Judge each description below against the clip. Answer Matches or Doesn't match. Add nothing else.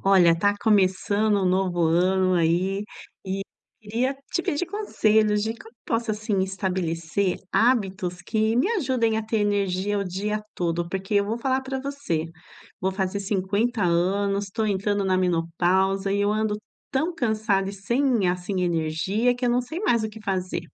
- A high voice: Matches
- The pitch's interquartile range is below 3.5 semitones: Matches